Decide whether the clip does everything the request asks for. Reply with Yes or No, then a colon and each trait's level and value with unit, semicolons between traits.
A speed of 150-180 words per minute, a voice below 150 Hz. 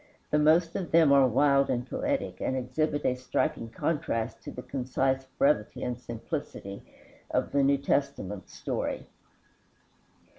No: average, 140 wpm; medium, 140 Hz